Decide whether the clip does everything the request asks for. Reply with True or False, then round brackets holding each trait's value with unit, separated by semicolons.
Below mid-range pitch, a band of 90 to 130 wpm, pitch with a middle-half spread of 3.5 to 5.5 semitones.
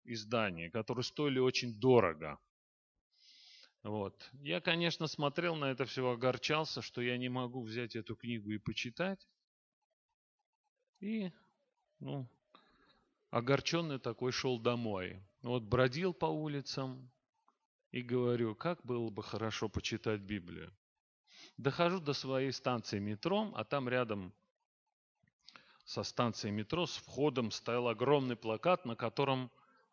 True (125 Hz; 115 wpm; 4.4 semitones)